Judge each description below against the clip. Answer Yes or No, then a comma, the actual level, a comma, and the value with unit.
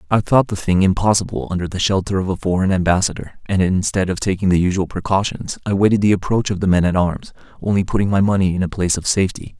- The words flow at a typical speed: No, fast, 230 wpm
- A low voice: Yes, very low, 95 Hz